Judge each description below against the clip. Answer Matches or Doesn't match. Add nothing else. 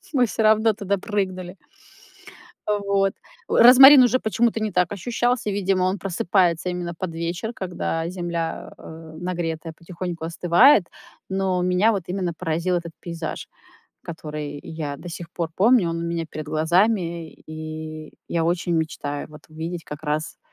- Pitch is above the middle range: Doesn't match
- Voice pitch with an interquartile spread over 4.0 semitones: Doesn't match